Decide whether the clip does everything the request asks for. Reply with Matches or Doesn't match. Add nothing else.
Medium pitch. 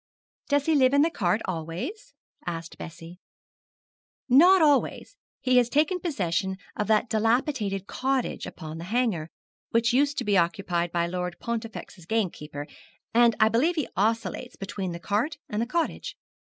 Doesn't match